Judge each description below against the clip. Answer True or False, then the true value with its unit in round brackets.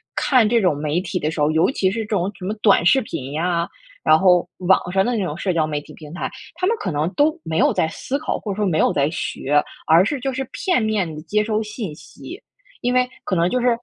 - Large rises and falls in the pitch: True (5.9 semitones)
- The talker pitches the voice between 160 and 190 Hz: True (185 Hz)